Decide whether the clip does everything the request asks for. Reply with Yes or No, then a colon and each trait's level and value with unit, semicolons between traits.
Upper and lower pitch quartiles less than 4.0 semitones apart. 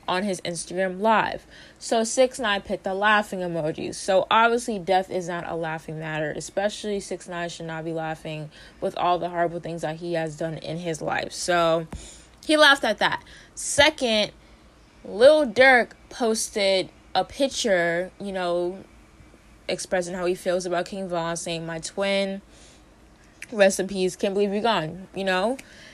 Yes: average, 3.5 semitones